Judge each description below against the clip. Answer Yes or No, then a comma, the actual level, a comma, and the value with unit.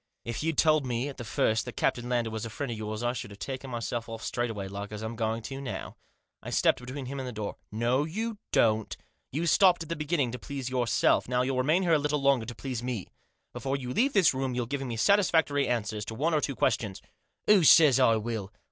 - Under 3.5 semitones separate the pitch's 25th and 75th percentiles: No, average, 4.1 semitones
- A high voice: No, low, 125 Hz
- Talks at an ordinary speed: No, fast, 240 wpm